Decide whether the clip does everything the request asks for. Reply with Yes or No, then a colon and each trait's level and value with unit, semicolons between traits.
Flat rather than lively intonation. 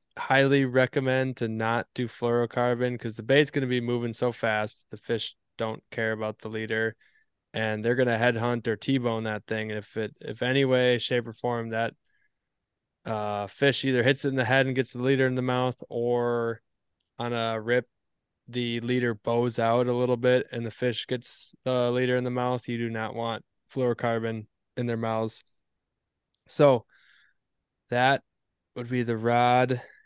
Yes: narrow, 1.9 semitones